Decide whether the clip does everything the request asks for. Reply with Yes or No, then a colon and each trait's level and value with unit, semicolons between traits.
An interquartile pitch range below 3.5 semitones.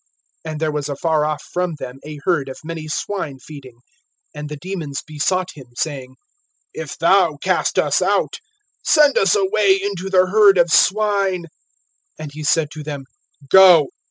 No: average, 4.3 semitones